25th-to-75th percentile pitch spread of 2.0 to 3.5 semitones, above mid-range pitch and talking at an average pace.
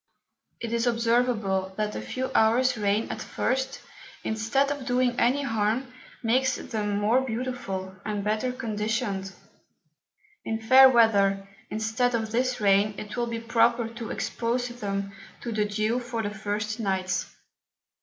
Yes: average, 2.8 semitones; high, 225 Hz; average, 145 wpm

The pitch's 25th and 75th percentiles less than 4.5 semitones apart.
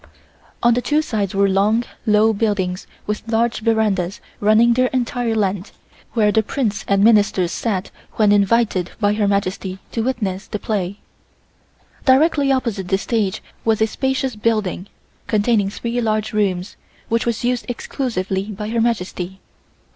Yes: average, 2.8 semitones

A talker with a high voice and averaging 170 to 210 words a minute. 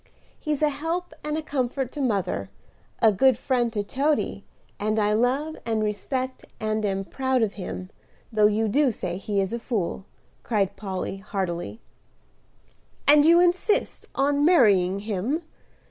No: high, 230 Hz; average, 145 wpm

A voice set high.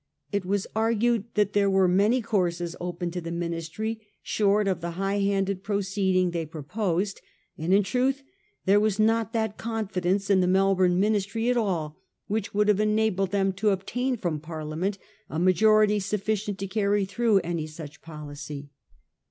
Yes: high, 195 Hz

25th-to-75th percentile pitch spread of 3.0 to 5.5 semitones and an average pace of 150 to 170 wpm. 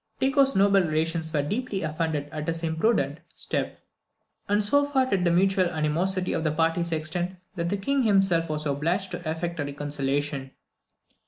Yes: average, 3.9 semitones; average, 165 wpm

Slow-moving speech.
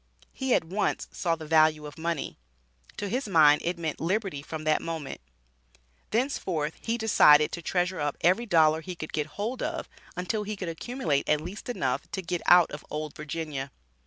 No: average, 185 wpm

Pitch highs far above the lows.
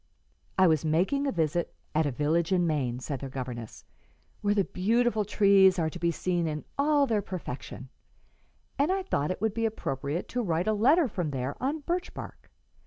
Yes: wide, 6.6 semitones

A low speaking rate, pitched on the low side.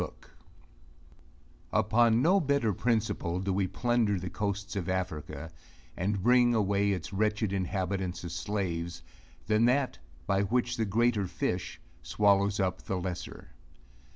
Yes: slow, 130 wpm; low, 100 Hz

